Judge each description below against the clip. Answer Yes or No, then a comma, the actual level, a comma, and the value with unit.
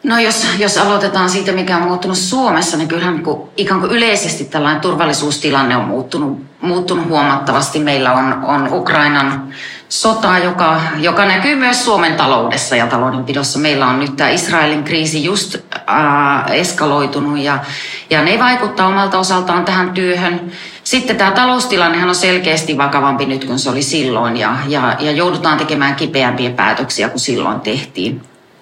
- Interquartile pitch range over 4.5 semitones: Yes, average, 4.9 semitones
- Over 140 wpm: Yes, average, 150 wpm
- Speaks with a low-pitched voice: No, medium, 160 Hz